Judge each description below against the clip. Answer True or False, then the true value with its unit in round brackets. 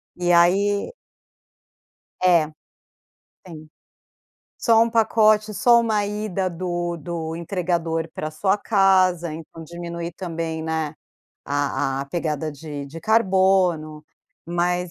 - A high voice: False (175 Hz)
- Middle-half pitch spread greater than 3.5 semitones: False (3.2 semitones)